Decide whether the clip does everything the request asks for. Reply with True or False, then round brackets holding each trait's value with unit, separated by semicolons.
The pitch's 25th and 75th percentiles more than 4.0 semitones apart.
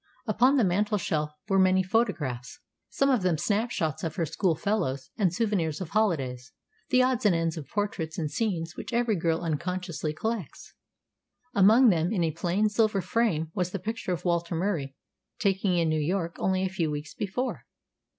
True (4.7 semitones)